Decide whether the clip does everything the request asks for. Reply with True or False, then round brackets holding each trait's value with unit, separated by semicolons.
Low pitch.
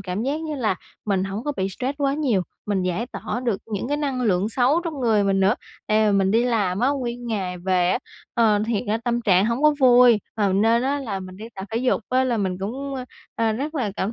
False (225 Hz)